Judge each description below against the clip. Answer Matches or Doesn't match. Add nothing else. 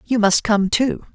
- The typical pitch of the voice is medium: Doesn't match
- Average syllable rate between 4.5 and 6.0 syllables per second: Doesn't match